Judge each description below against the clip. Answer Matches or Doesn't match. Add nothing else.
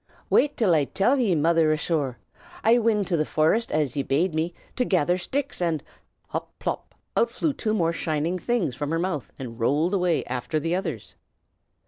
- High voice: Doesn't match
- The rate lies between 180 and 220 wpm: Matches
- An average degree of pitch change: Matches